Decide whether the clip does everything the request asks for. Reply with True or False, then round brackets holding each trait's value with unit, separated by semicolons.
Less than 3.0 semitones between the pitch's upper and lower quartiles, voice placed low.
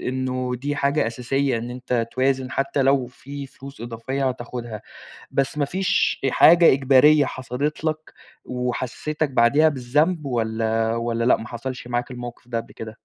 True (2.6 semitones; 130 Hz)